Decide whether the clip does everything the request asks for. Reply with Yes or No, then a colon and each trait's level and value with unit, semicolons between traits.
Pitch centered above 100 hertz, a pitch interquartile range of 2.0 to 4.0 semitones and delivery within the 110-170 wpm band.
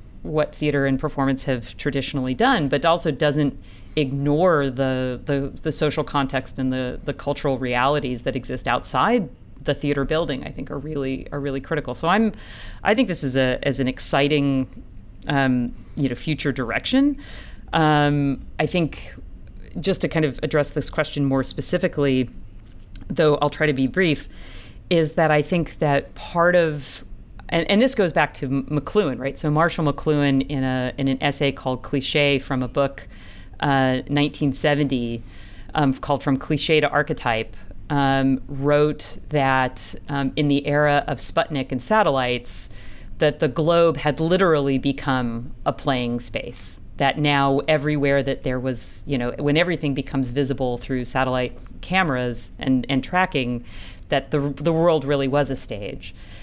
Yes: medium, 140 Hz; average, 2.7 semitones; average, 160 wpm